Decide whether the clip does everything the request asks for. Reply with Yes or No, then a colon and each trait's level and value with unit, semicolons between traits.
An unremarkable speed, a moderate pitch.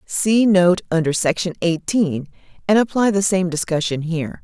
Yes: average, 150 wpm; medium, 180 Hz